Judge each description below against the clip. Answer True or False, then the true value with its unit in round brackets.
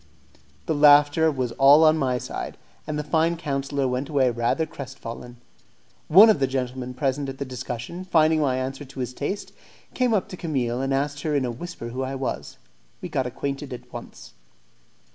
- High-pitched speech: False (135 Hz)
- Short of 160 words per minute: False (185 wpm)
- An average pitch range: True (3.2 semitones)